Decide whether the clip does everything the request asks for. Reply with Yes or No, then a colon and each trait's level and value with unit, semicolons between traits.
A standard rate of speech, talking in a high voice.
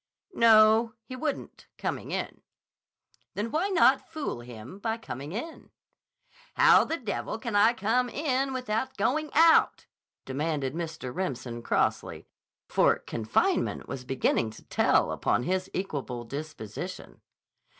No: slow, 125 wpm; high, 205 Hz